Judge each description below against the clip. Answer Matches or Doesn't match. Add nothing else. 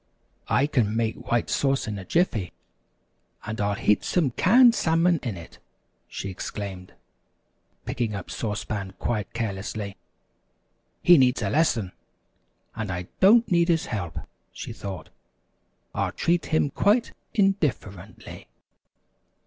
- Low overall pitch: Matches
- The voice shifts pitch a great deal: Matches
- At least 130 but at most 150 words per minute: Matches